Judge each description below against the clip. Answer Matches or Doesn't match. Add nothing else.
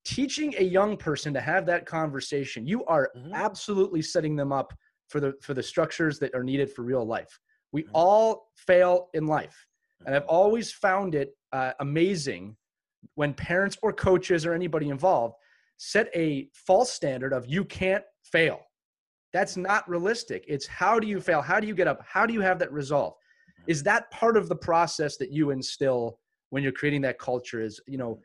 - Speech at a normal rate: Matches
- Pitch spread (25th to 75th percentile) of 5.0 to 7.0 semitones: Matches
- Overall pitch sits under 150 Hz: Doesn't match